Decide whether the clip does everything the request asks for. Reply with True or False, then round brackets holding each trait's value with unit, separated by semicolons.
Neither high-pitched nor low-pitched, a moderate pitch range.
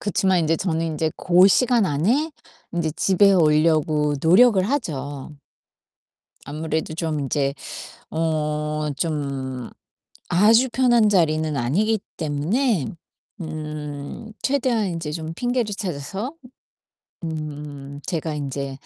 True (160 Hz; 4.9 semitones)